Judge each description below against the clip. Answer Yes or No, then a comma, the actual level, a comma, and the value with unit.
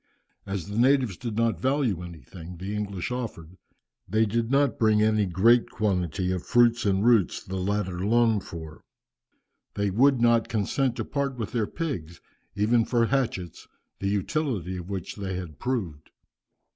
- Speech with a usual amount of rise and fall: Yes, average, 4.3 semitones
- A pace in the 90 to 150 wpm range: No, average, 160 wpm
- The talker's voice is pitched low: Yes, low, 105 Hz